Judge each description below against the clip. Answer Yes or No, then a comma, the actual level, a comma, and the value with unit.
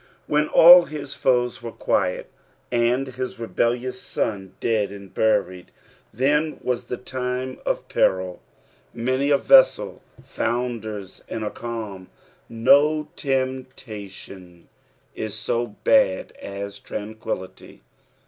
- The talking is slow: Yes, slow, 110 wpm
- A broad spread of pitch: No, average, 4.1 semitones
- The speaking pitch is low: Yes, low, 120 Hz